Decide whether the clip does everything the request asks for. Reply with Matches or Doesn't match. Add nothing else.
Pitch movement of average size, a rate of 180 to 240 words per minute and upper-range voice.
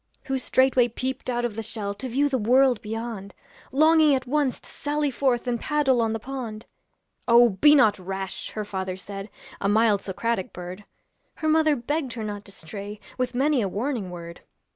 Matches